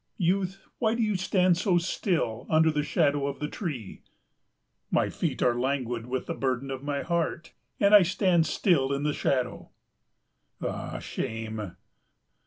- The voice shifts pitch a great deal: Yes, wide, 5.9 semitones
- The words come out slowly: No, average, 155 wpm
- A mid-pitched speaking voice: Yes, medium, 150 Hz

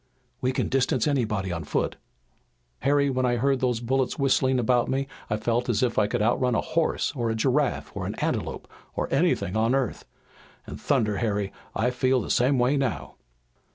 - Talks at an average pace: Yes, average, 190 wpm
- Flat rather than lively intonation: No, average, 3.0 semitones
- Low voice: Yes, low, 125 Hz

